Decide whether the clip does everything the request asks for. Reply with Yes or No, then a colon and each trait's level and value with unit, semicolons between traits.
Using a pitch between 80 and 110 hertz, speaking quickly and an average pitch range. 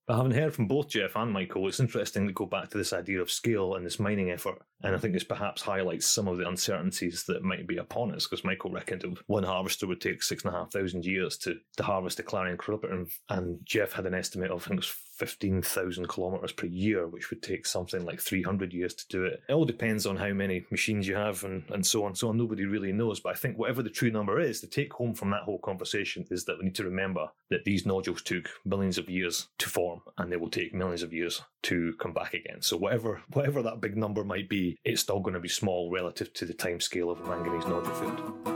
Yes: very low, 95 Hz; fast, 250 wpm; average, 3.0 semitones